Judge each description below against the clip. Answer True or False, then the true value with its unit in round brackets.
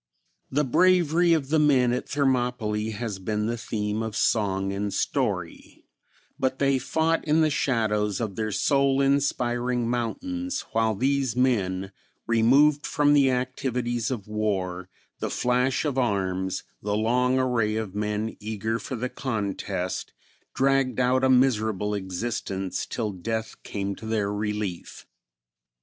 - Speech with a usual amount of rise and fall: True (4.1 semitones)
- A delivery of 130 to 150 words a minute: True (135 wpm)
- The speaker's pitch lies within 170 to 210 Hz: False (115 Hz)